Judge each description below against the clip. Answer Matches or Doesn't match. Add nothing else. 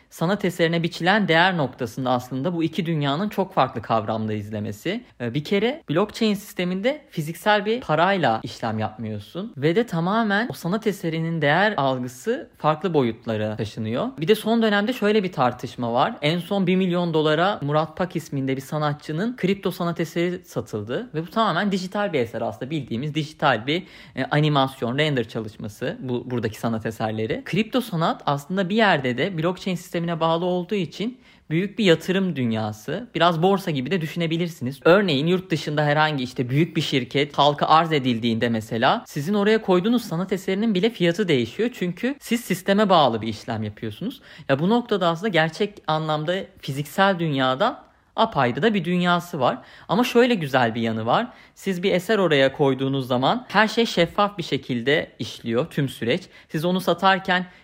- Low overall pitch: Doesn't match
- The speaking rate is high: Matches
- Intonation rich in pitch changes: Matches